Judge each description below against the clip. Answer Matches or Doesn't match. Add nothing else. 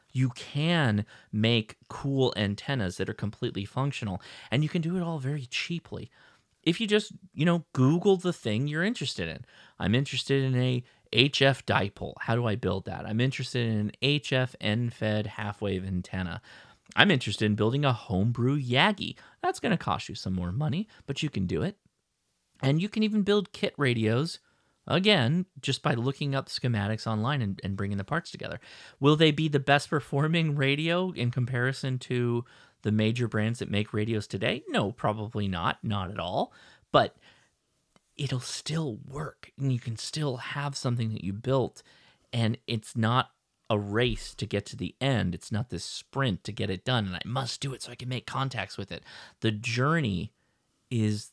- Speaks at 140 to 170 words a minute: Doesn't match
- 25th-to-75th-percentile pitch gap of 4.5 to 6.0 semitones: Matches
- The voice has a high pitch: Doesn't match